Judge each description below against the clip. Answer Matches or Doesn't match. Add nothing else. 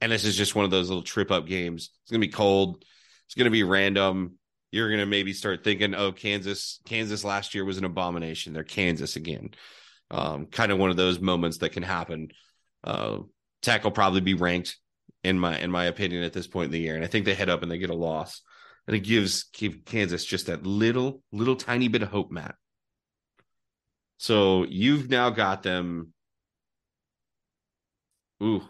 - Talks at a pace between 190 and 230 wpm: Matches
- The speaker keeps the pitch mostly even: Doesn't match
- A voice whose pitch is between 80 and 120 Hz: Matches